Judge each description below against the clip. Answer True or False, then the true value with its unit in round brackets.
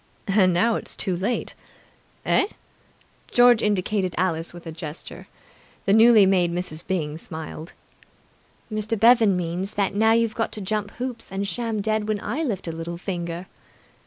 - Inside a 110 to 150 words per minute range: False (160 wpm)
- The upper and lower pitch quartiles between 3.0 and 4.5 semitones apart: True (4.1 semitones)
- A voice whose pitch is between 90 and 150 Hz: False (195 Hz)